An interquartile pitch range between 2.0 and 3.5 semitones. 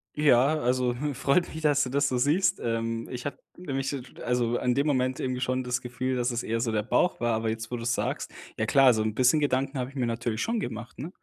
Yes: average, 2.8 semitones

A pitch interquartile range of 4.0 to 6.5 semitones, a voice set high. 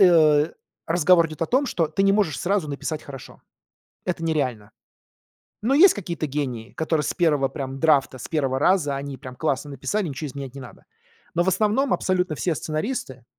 No: average, 4.7 semitones; medium, 155 Hz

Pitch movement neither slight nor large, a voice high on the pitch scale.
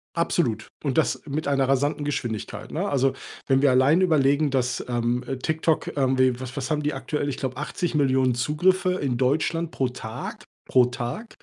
No: average, 3.1 semitones; low, 135 Hz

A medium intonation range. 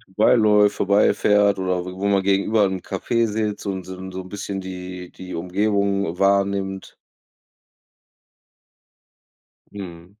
No: narrow, 1.7 semitones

